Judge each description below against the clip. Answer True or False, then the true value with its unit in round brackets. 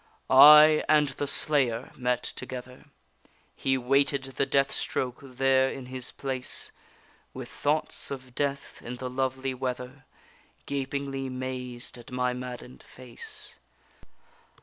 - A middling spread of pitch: False (1.5 semitones)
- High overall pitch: False (130 Hz)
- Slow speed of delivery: True (120 wpm)